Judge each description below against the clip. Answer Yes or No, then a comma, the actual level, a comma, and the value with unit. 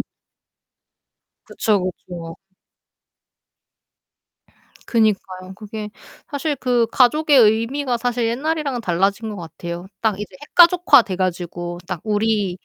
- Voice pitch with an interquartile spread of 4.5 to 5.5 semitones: Yes, average, 5.1 semitones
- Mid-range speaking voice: No, high, 215 Hz